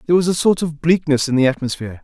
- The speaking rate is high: Yes, fast, 265 wpm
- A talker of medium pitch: Yes, medium, 150 Hz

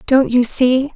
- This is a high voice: Yes, very high, 255 Hz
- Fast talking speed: No, average, 190 wpm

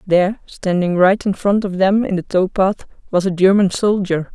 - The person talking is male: No, female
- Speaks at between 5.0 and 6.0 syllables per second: No, 4.8 syllables/s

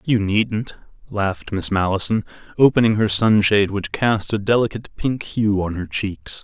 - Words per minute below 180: Yes, average, 160 wpm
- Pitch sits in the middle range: No, low, 105 Hz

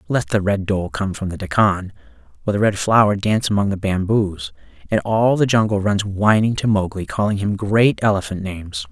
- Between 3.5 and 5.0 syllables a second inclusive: No, 5.4 syllables/s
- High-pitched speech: No, low, 100 Hz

